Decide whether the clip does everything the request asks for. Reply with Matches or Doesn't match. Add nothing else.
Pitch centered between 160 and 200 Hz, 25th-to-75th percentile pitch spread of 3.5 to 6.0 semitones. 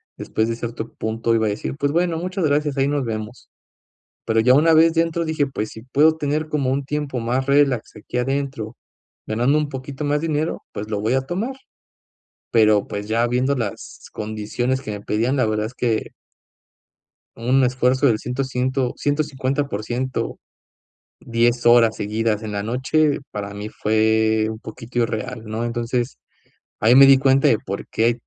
Doesn't match